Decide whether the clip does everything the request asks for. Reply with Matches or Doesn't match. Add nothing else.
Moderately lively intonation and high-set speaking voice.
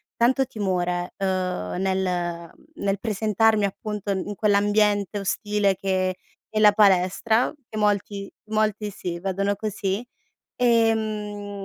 Doesn't match